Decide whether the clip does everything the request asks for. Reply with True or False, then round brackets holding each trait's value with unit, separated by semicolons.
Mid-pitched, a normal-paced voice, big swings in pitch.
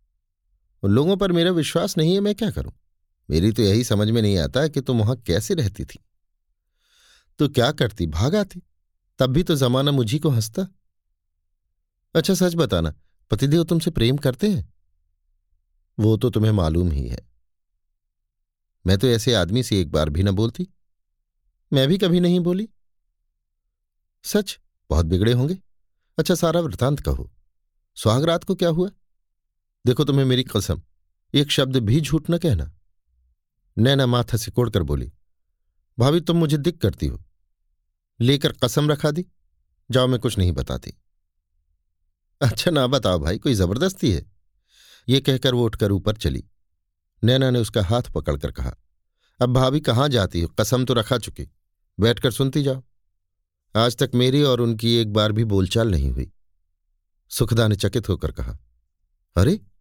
False (110 Hz; 155 wpm; 8.7 semitones)